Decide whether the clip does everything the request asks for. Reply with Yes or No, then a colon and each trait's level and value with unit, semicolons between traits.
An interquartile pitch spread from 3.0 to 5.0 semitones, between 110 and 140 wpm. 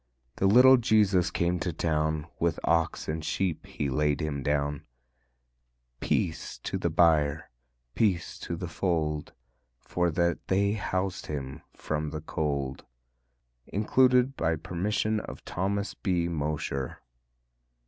Yes: average, 4.0 semitones; slow, 135 wpm